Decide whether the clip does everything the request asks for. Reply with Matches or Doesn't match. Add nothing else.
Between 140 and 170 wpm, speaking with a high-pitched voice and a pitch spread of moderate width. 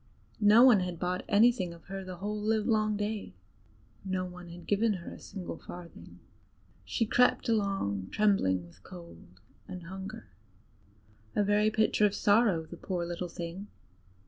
Matches